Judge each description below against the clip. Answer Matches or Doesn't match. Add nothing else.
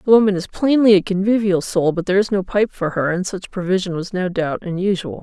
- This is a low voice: Doesn't match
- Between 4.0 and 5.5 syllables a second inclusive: Doesn't match